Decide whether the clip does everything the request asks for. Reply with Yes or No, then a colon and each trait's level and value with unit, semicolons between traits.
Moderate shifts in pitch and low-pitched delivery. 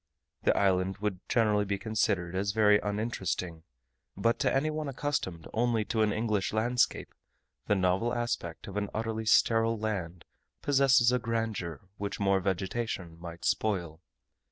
Yes: average, 3.6 semitones; low, 105 Hz